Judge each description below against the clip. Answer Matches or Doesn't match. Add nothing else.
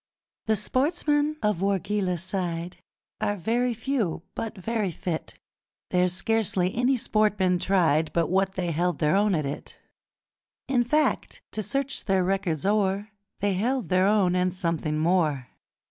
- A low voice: Doesn't match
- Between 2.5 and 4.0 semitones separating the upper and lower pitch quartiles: Matches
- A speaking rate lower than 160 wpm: Matches